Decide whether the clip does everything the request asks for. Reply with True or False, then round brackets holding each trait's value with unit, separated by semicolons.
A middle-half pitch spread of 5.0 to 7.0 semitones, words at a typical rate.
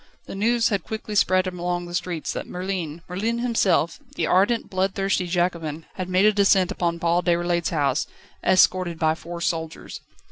False (2.4 semitones; 165 wpm)